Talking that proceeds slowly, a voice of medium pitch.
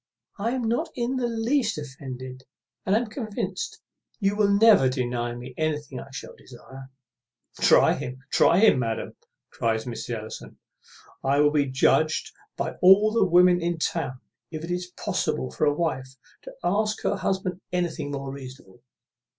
No: average, 160 wpm; medium, 155 Hz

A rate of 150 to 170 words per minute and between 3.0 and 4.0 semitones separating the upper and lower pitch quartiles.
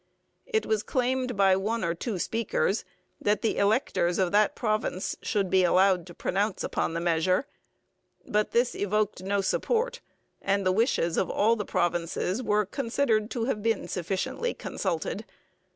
Yes: average, 155 wpm; average, 3.6 semitones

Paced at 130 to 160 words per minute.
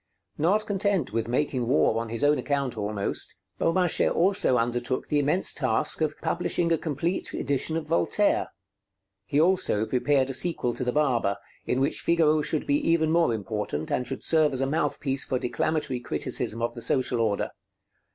No: average, 170 wpm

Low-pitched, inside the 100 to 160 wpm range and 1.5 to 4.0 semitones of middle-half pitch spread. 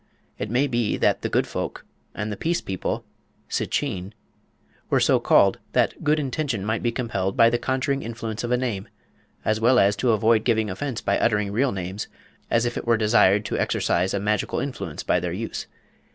No: low, 115 Hz; average, 195 wpm; average, 3.3 semitones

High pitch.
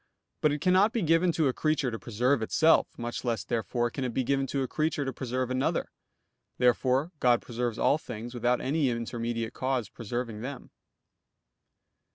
No: low, 125 Hz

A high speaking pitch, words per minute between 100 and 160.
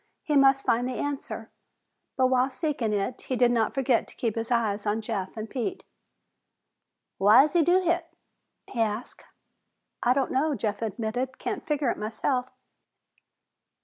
Yes: very high, 250 Hz; average, 155 wpm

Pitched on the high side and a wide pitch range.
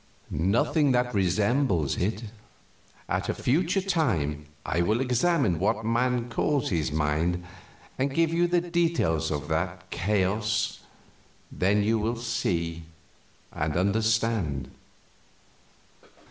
No: low, 110 Hz; wide, 6.7 semitones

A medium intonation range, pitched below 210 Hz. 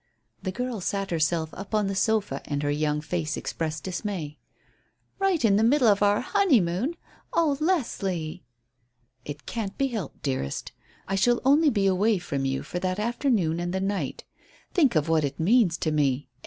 No: wide, 6.4 semitones; high, 190 Hz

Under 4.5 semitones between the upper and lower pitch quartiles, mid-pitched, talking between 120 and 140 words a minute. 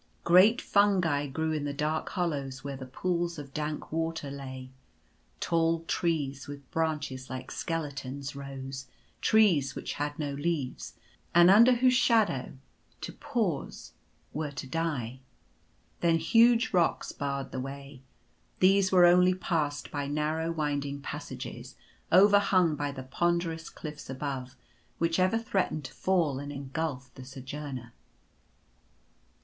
Yes: average, 3.8 semitones; medium, 150 Hz; slow, 135 wpm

